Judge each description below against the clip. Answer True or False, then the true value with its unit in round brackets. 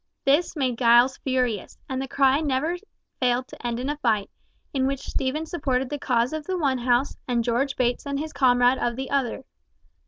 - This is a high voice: True (260 Hz)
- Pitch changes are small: True (2.3 semitones)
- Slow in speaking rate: False (195 wpm)